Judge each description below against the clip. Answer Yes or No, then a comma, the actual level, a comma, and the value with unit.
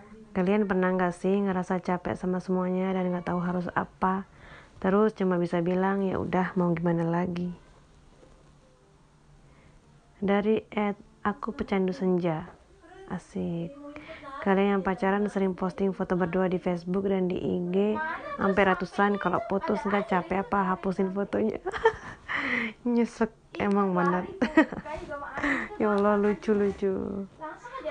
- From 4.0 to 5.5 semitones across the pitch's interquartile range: No, narrow, 2.4 semitones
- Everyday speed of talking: Yes, average, 125 wpm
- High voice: Yes, high, 195 Hz